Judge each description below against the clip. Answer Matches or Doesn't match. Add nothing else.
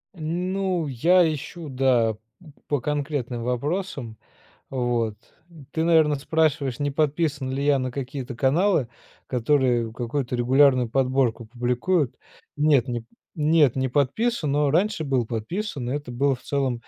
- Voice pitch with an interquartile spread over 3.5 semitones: Matches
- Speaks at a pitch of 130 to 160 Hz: Matches